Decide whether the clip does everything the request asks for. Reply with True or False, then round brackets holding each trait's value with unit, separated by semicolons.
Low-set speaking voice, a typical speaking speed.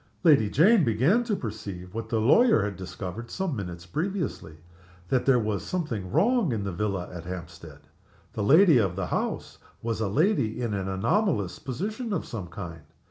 True (110 Hz; 175 wpm)